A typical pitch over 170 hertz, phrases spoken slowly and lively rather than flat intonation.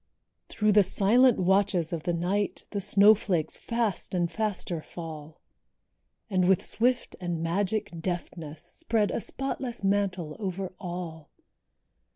No: high, 190 Hz; slow, 125 wpm; average, 3.4 semitones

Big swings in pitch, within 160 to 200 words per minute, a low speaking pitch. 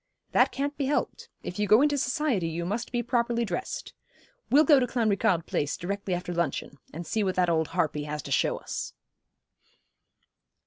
No: wide, 6.8 semitones; average, 180 wpm; high, 205 Hz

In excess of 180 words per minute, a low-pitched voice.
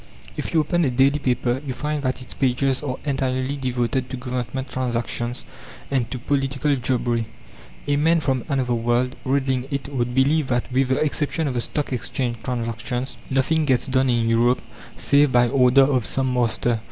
No: average, 175 wpm; low, 130 Hz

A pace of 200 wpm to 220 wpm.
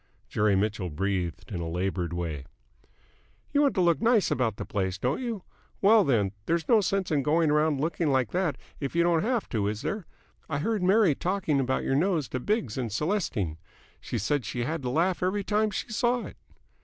Yes: fast, 205 wpm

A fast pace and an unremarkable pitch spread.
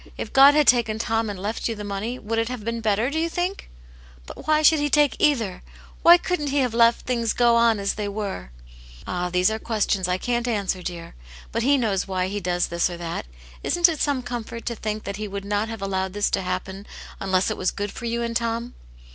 Yes: fast, 250 wpm; average, 4.1 semitones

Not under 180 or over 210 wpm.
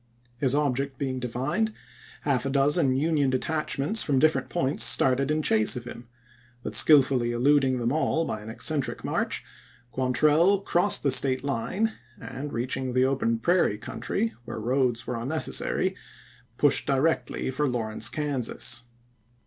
No: average, 145 wpm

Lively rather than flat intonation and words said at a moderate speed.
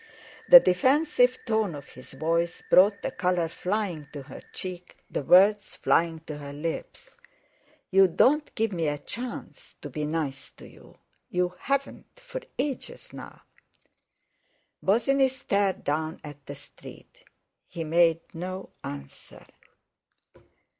No: wide, 6.2 semitones; slow, 130 wpm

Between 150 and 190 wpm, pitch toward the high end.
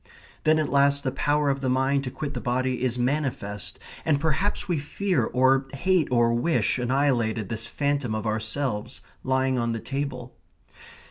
No: average, 170 wpm; low, 135 Hz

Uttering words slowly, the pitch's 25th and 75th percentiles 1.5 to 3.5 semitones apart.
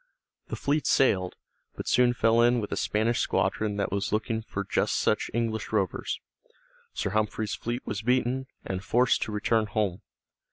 No: average, 165 wpm; average, 2.7 semitones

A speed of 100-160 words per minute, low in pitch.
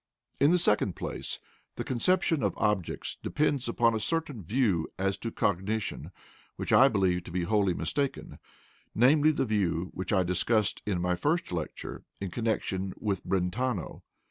Yes: average, 155 wpm; low, 105 Hz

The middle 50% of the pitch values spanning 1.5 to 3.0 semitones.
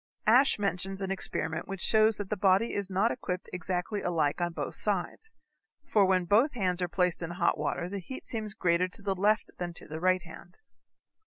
Yes: average, 2.7 semitones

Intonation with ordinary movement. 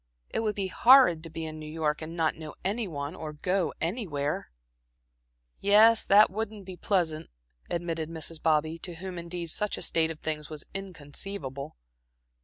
Yes: average, 3.9 semitones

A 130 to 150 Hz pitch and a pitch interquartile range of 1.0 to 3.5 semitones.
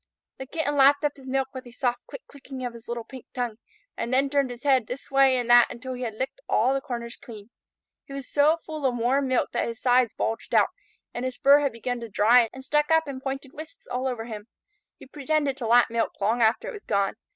No: very high, 255 Hz; narrow, 2.6 semitones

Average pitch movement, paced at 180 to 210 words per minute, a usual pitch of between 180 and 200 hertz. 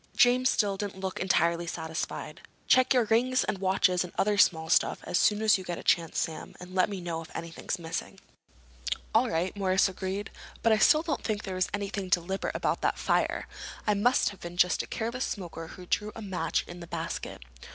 Yes: average, 3.2 semitones; fast, 205 wpm; high, 190 Hz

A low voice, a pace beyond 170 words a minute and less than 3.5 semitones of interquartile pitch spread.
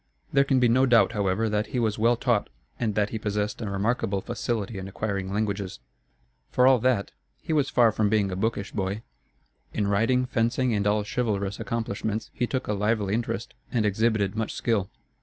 Yes: low, 110 Hz; average, 190 wpm; average, 2.7 semitones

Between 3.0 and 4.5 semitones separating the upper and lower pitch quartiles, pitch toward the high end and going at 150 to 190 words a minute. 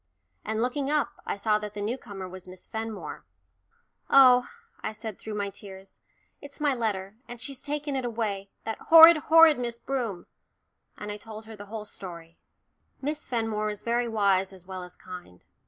Yes: average, 4.0 semitones; high, 220 Hz; average, 180 wpm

